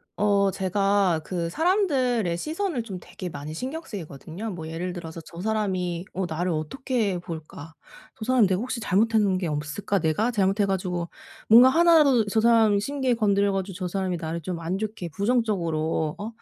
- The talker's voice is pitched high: Yes, high, 195 Hz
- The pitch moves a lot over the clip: No, average, 4.8 semitones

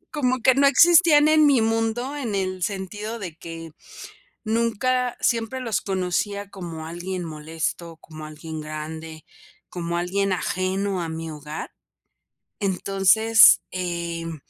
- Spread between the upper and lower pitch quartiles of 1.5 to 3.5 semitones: No, wide, 5.5 semitones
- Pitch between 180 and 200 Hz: Yes, high, 190 Hz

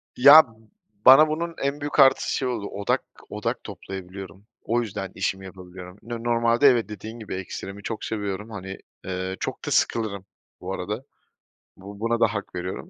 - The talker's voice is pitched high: No, low, 105 Hz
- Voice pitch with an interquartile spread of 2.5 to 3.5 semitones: No, average, 3.9 semitones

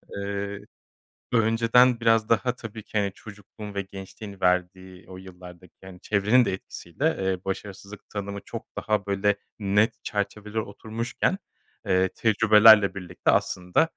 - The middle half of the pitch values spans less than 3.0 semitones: Yes, narrow, 2.6 semitones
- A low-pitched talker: Yes, low, 100 Hz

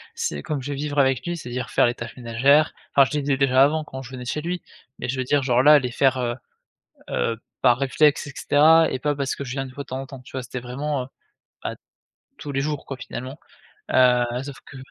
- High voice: No, low, 135 Hz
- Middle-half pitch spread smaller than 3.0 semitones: Yes, narrow, 2.4 semitones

